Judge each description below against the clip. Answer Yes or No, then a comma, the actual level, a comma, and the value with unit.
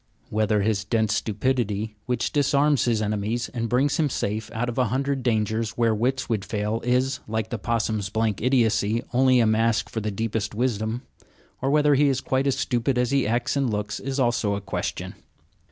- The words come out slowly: No, average, 190 wpm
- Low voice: Yes, low, 115 Hz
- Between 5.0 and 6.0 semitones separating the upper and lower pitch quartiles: No, average, 3.3 semitones